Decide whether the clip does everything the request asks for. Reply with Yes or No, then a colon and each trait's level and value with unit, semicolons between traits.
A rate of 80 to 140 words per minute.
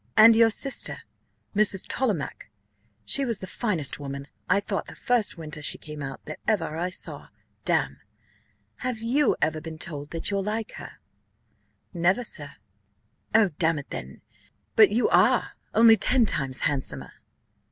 No: average, 150 wpm